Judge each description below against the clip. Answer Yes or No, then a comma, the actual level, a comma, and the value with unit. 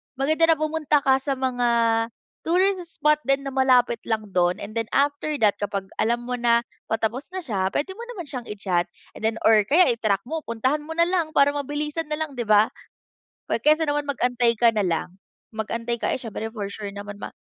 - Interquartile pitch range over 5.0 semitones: Yes, wide, 5.5 semitones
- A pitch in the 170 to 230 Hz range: No, very high, 250 Hz